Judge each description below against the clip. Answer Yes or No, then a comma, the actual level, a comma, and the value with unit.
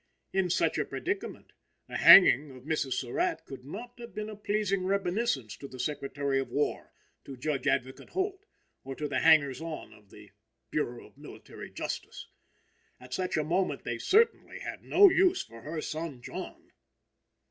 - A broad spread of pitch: Yes, wide, 7.7 semitones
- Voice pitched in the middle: Yes, medium, 155 Hz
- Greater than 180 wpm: No, average, 170 wpm